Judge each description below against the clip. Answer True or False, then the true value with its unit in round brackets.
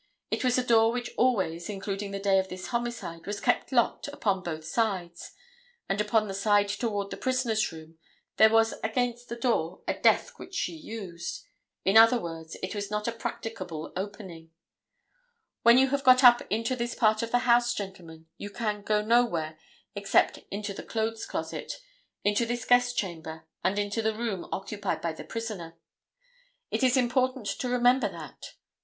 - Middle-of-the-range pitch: False (215 Hz)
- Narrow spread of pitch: False (3.9 semitones)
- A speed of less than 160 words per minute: False (175 wpm)